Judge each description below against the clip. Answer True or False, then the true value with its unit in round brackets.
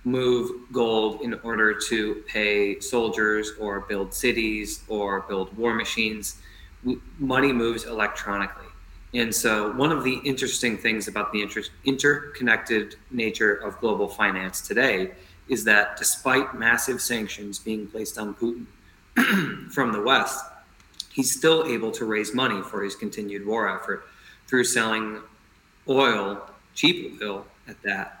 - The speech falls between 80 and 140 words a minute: True (135 wpm)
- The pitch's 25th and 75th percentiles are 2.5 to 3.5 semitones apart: True (2.8 semitones)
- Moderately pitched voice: False (110 Hz)